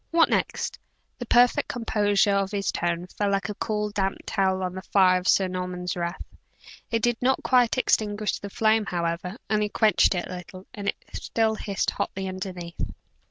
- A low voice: No, high, 200 Hz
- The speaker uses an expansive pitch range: No, average, 2.9 semitones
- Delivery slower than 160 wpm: No, average, 180 wpm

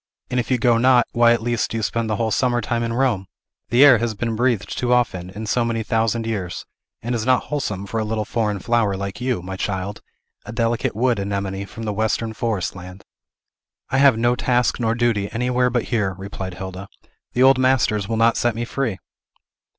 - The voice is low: Yes, low, 115 Hz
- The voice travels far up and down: No, average, 3.1 semitones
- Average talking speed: No, fast, 210 wpm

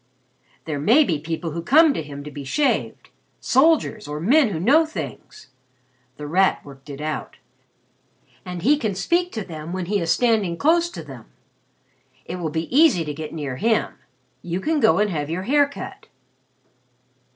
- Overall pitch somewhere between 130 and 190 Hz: Yes, medium, 185 Hz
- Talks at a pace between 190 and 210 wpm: No, average, 175 wpm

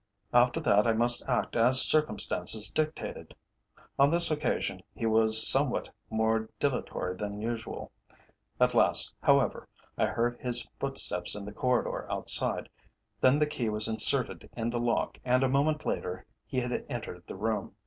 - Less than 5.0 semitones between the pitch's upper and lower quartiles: Yes, average, 3.0 semitones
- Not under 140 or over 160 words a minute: Yes, average, 155 wpm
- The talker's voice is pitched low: Yes, low, 120 Hz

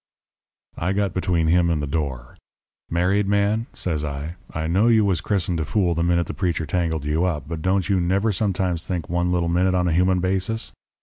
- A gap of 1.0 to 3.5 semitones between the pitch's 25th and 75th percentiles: Yes, narrow, 2.6 semitones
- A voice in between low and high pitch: No, very low, 90 Hz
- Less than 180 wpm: No, fast, 205 wpm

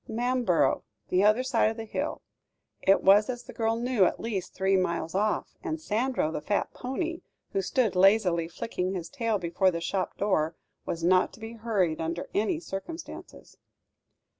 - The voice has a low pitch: No, high, 210 Hz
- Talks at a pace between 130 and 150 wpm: No, average, 170 wpm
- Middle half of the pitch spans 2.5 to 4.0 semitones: No, average, 4.5 semitones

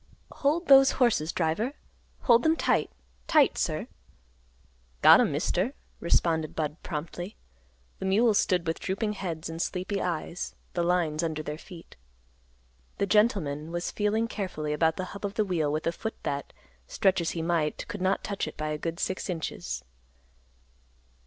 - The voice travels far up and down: No, average, 4.4 semitones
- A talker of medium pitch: Yes, medium, 175 Hz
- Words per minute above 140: Yes, average, 160 wpm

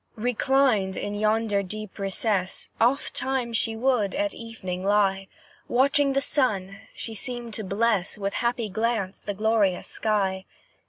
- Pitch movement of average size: Yes, average, 3.4 semitones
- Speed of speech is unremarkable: No, slow, 130 wpm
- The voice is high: Yes, high, 215 Hz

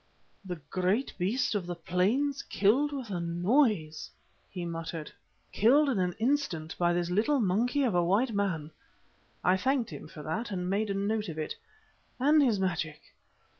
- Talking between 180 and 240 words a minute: No, average, 170 wpm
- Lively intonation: Yes, wide, 5.8 semitones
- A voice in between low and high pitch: No, high, 195 Hz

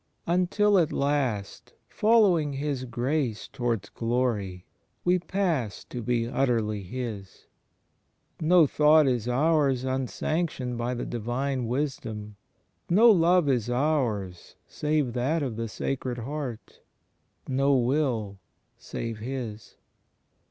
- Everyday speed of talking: No, slow, 110 wpm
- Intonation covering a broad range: No, average, 4.5 semitones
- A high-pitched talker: No, low, 130 Hz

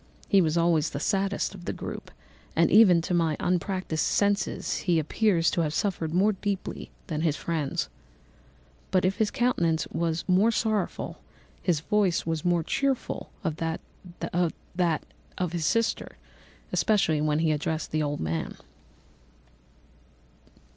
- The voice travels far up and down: No, average, 3.7 semitones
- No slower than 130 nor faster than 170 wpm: Yes, average, 140 wpm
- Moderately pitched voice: Yes, medium, 170 Hz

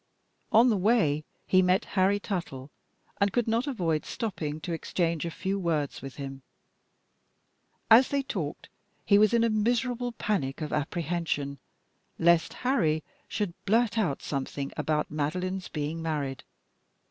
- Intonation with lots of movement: Yes, wide, 6.0 semitones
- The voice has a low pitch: No, medium, 175 Hz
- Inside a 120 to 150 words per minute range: Yes, average, 140 wpm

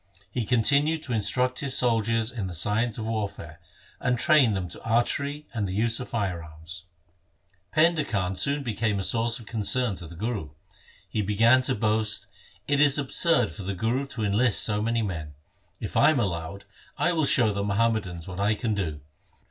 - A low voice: Yes, low, 110 Hz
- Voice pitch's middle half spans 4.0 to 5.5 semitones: Yes, average, 4.3 semitones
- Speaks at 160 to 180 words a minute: No, average, 190 wpm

